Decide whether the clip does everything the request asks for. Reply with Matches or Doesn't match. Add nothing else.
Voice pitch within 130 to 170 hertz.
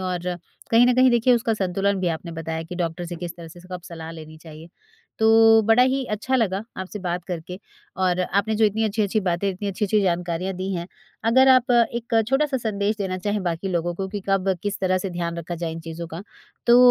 Doesn't match